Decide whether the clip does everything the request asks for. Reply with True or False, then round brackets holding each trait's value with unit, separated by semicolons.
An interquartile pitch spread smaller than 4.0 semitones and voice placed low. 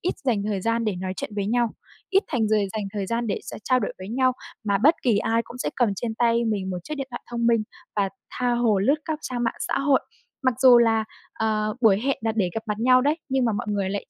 False (3.1 semitones; 230 Hz)